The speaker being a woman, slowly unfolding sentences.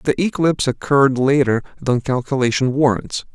No: male; slow, 125 wpm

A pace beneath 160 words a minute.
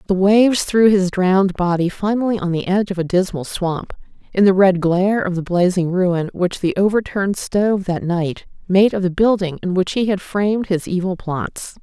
No: fast, 205 wpm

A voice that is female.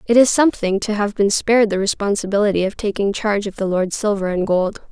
Yes: female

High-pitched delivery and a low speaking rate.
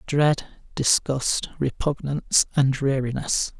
No: low, 135 Hz; slow, 85 wpm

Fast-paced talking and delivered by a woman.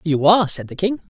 No: fast, 255 wpm; male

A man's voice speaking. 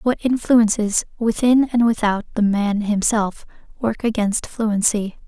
No: female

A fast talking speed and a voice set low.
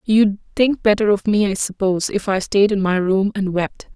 No: fast, 230 wpm; high, 200 Hz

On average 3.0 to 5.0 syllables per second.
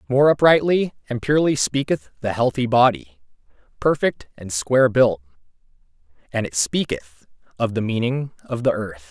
Yes: 4.9 syllables/s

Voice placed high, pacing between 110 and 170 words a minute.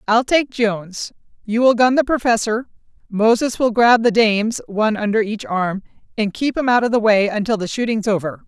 No: high, 220 Hz; average, 200 wpm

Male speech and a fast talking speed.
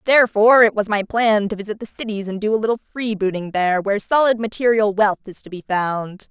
No: female; fast, 220 wpm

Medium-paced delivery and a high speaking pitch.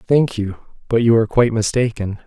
No: average, 185 wpm; low, 115 Hz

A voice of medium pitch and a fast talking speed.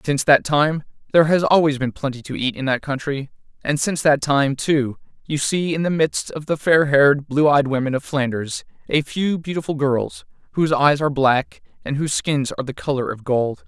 Yes: medium, 145 Hz; fast, 210 wpm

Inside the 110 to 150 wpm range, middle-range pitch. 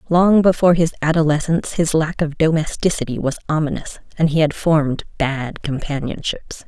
Yes: average, 145 wpm; medium, 155 Hz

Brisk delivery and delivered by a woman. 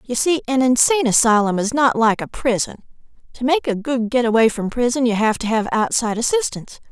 Yes: fast, 210 wpm; female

